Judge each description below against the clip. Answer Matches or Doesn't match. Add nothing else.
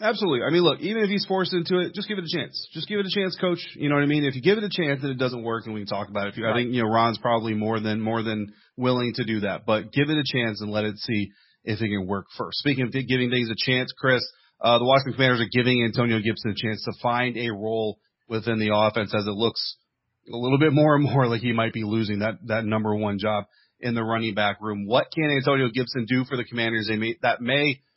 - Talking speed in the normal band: Doesn't match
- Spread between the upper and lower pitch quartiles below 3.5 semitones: Doesn't match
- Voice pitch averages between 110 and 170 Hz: Matches